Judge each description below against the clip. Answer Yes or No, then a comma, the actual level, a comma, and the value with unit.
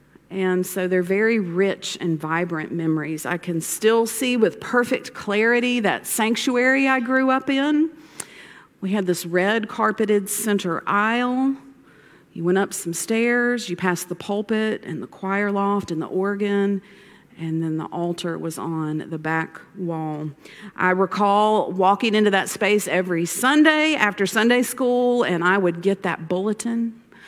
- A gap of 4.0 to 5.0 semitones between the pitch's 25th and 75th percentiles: Yes, average, 4.6 semitones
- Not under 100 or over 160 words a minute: Yes, average, 155 wpm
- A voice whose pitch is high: Yes, high, 200 Hz